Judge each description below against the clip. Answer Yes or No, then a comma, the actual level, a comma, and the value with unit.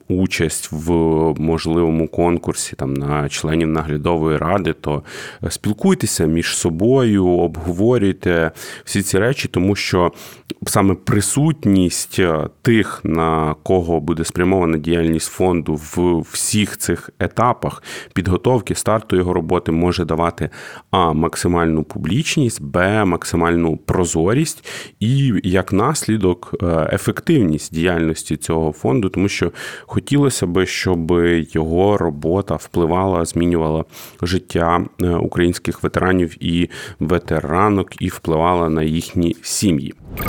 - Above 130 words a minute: No, slow, 105 wpm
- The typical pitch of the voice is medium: No, very low, 85 Hz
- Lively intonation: No, average, 3.1 semitones